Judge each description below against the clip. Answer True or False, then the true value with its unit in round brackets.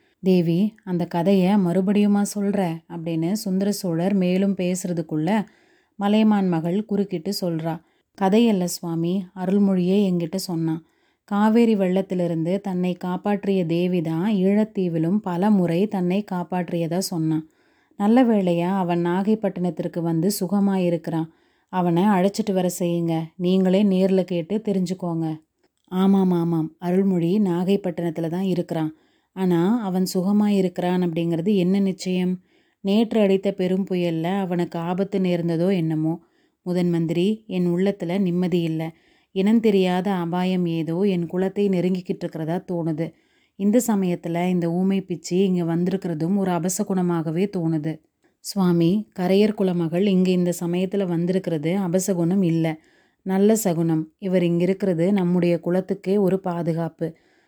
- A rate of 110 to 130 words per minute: True (115 wpm)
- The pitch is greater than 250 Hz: False (185 Hz)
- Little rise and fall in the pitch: True (2.3 semitones)